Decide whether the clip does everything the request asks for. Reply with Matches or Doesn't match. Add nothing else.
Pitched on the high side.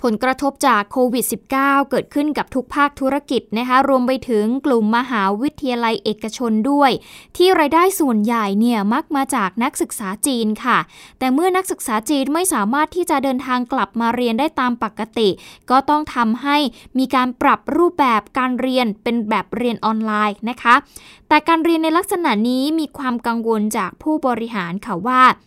Matches